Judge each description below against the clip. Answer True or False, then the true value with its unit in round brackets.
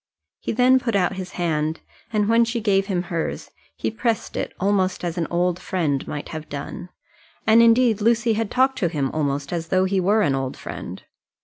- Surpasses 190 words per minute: True (200 wpm)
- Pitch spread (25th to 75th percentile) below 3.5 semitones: False (5.4 semitones)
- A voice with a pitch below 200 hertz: True (190 Hz)